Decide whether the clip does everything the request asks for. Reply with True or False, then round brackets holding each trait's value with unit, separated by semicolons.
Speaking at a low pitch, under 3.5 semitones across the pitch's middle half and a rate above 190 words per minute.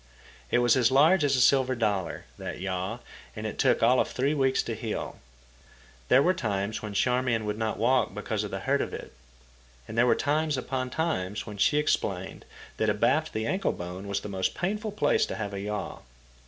False (115 Hz; 4.5 semitones; 205 wpm)